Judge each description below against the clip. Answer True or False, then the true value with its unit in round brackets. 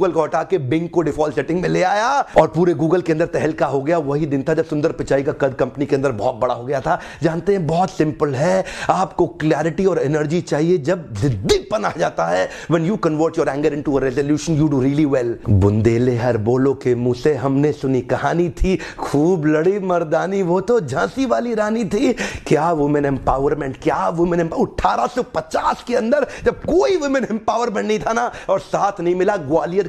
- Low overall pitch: False (160 Hz)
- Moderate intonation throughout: True (4.3 semitones)